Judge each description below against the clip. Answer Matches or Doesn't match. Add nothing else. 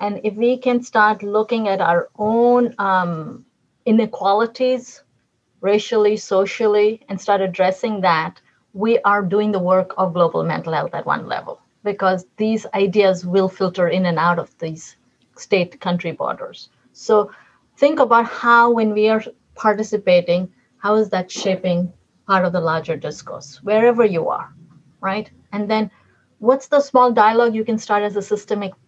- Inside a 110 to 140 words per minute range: Doesn't match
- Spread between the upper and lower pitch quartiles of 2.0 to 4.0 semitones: Matches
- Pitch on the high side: Matches